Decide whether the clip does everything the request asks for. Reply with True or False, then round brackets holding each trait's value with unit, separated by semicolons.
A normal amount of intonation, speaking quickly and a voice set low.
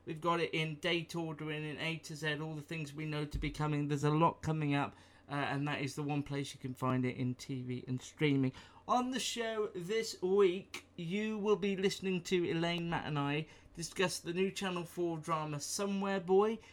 False (4.3 semitones; 215 wpm; 160 Hz)